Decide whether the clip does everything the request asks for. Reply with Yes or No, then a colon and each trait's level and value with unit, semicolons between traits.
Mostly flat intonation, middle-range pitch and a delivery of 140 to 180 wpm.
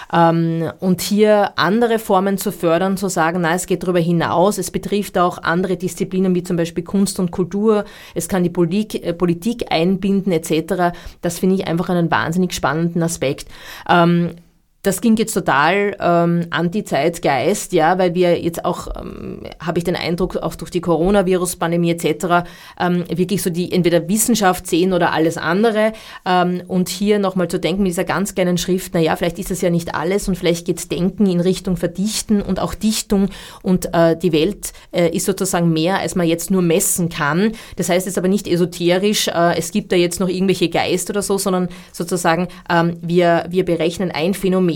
No: narrow, 2.1 semitones; medium, 180 Hz; fast, 190 wpm